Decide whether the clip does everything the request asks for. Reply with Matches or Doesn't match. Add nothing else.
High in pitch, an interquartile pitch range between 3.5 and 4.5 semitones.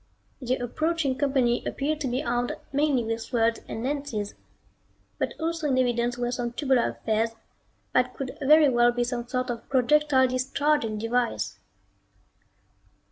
Doesn't match